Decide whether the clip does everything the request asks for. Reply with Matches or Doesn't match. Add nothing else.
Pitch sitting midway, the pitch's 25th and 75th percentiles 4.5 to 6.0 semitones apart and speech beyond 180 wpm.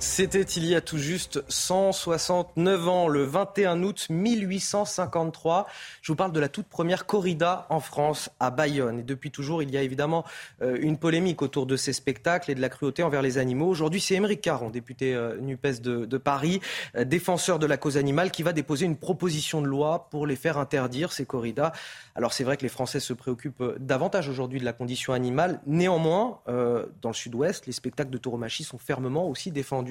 Matches